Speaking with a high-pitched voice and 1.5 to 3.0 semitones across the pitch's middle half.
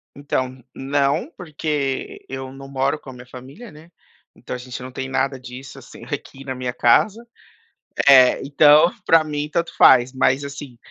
No: low, 135 Hz; narrow, 2.4 semitones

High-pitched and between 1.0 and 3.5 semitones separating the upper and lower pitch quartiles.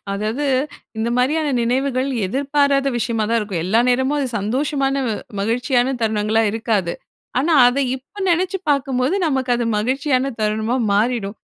No: very high, 250 Hz; average, 3.9 semitones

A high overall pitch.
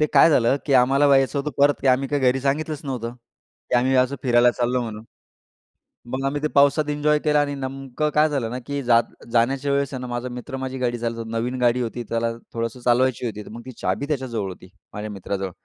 No: low, 130 Hz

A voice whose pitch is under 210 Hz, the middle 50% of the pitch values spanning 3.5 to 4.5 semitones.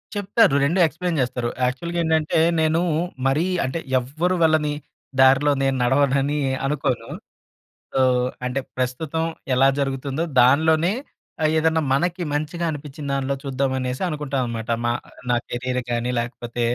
Yes: medium, 140 Hz; average, 3.8 semitones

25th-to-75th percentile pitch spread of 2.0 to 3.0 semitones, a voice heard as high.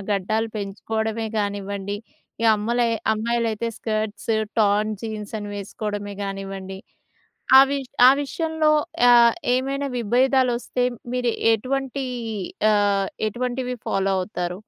No: average, 3.4 semitones; high, 220 Hz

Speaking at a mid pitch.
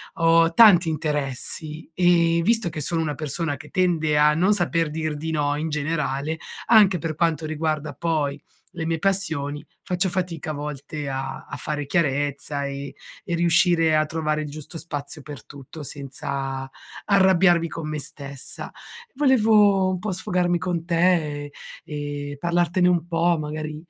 Yes: medium, 160 Hz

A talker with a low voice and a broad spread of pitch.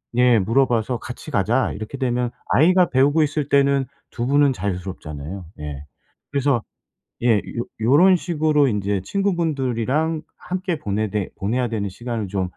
Yes: low, 125 Hz; wide, 5.9 semitones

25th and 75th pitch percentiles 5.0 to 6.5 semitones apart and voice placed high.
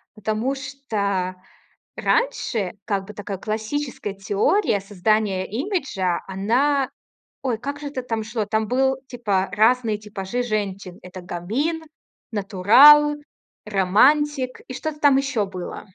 Yes: wide, 5.5 semitones; high, 220 Hz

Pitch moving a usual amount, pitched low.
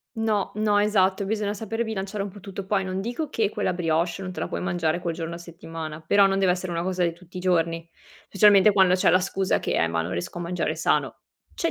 No: average, 3.0 semitones; medium, 185 Hz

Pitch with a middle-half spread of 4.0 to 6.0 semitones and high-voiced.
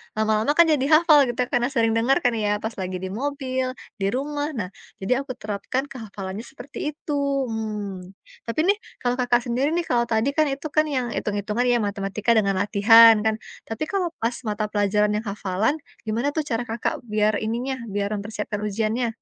No: average, 3.6 semitones; high, 225 Hz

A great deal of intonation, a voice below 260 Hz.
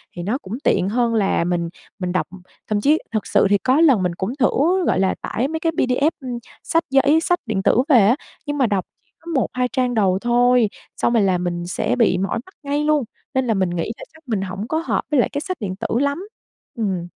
Yes: wide, 6.6 semitones; high, 235 Hz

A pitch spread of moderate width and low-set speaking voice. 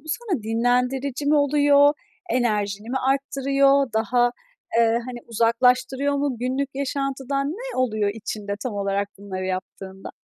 No: average, 4.0 semitones; very high, 255 Hz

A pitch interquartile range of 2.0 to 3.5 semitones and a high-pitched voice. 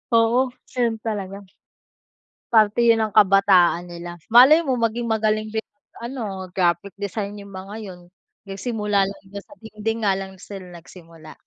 Yes: average, 2.8 semitones; high, 205 Hz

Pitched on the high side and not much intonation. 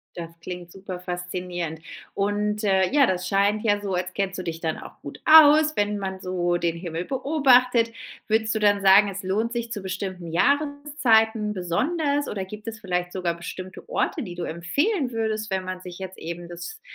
No: high, 195 Hz; average, 4.1 semitones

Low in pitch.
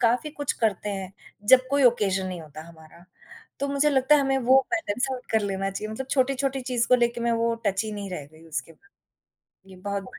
No: high, 225 Hz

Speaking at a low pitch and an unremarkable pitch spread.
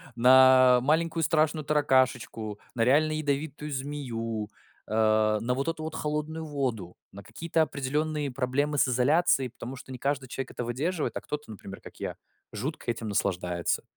Yes: low, 130 Hz; average, 4.5 semitones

